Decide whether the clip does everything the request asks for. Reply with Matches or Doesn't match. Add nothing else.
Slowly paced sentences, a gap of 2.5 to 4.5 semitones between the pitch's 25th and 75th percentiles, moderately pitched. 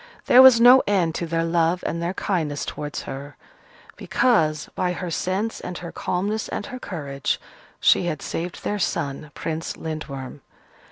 Doesn't match